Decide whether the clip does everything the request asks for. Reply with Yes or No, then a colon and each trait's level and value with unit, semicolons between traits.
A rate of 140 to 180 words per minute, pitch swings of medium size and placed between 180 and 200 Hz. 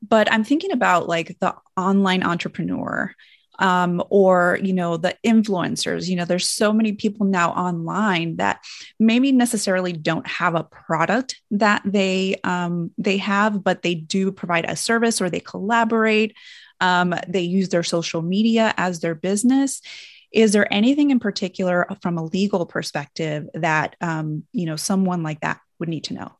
Yes: average, 165 wpm; average, 3.8 semitones; high, 190 Hz